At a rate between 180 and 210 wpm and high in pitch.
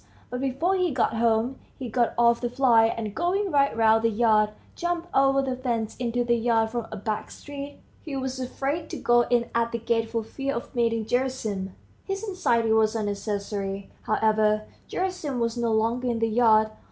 Yes: average, 190 wpm; high, 235 Hz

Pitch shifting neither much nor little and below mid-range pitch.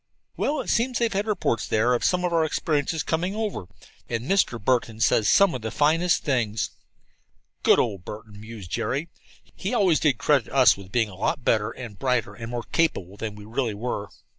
No: wide, 7.3 semitones; low, 125 Hz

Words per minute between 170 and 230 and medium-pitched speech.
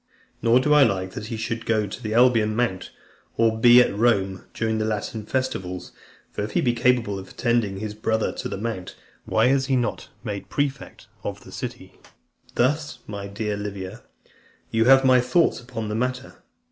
No: average, 185 wpm; low, 115 Hz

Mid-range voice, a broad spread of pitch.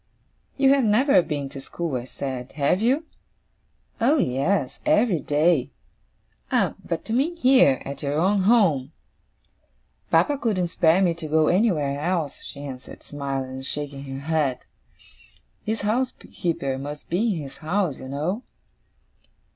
Yes: medium, 160 Hz; wide, 6.9 semitones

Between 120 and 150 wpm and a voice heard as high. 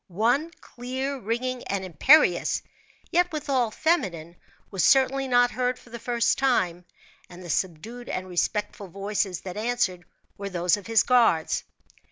Yes: average, 145 wpm; high, 225 Hz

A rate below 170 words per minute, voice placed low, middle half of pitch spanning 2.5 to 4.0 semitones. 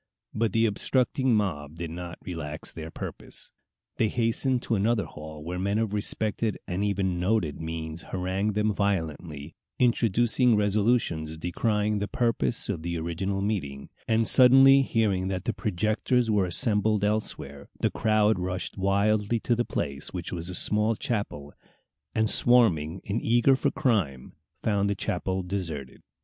No: average, 150 wpm; low, 100 Hz; average, 4.5 semitones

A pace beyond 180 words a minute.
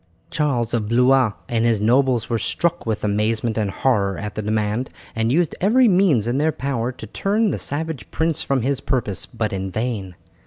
Yes: average, 190 wpm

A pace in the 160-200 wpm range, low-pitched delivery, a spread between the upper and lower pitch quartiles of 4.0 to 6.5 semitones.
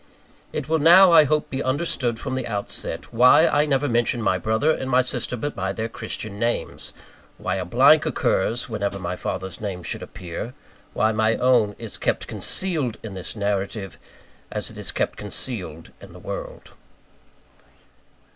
Yes: average, 165 wpm; low, 115 Hz; average, 4.8 semitones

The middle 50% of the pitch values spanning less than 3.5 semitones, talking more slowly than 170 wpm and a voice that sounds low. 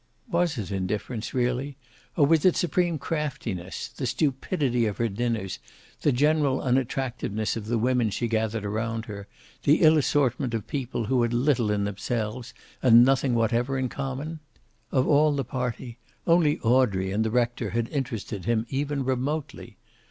No: average, 3.8 semitones; average, 160 wpm; low, 125 Hz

